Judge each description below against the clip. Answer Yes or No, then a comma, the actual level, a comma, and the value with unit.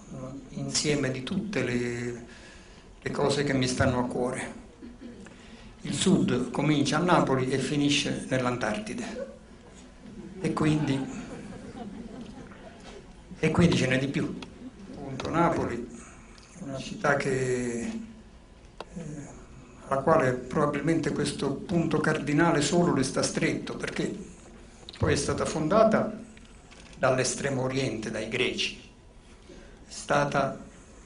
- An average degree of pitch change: No, wide, 6.8 semitones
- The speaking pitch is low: No, medium, 150 Hz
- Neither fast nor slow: No, slow, 105 wpm